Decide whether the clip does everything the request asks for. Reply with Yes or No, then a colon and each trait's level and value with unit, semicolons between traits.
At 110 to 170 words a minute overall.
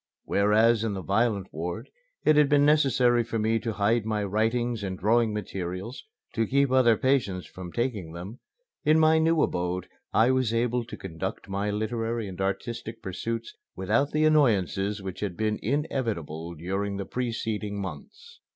Yes: average, 160 wpm